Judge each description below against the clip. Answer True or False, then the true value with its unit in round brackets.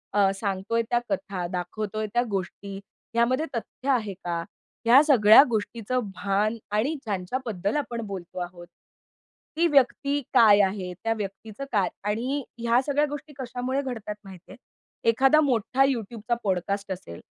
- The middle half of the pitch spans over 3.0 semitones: True (4.5 semitones)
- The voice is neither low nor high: False (220 Hz)